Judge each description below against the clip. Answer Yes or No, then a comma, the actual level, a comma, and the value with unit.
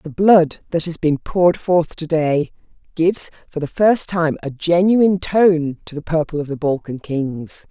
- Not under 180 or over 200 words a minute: Yes, average, 185 wpm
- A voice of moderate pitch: Yes, medium, 165 Hz